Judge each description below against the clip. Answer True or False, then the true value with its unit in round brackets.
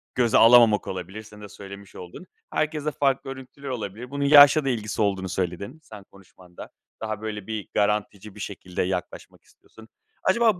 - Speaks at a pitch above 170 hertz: False (110 Hz)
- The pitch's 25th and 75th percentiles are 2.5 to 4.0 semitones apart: False (5.3 semitones)